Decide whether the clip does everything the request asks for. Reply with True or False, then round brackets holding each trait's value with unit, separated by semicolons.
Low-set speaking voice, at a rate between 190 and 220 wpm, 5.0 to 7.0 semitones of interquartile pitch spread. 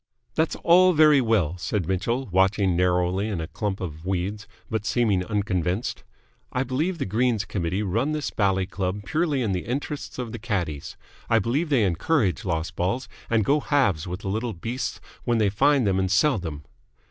False (105 Hz; 180 wpm; 5.5 semitones)